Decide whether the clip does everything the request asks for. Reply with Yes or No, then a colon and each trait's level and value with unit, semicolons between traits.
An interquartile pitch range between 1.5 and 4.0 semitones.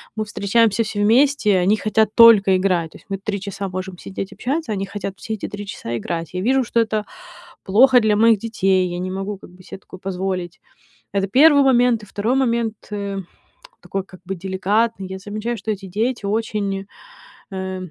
Yes: average, 2.9 semitones